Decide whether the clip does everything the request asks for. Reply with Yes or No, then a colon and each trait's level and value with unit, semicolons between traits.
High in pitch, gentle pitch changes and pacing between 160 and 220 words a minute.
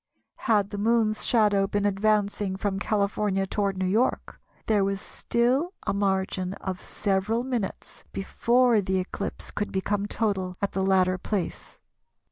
No: high, 200 Hz; narrow, 2.0 semitones; average, 140 wpm